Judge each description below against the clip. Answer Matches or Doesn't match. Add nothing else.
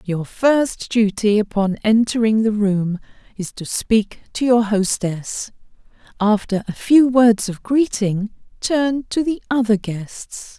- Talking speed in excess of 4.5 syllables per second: Doesn't match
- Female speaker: Matches